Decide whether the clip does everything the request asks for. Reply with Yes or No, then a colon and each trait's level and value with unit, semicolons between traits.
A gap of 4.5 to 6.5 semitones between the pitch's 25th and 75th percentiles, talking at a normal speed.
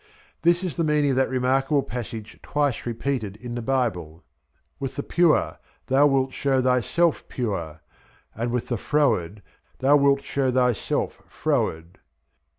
No: average, 3.7 semitones; average, 145 wpm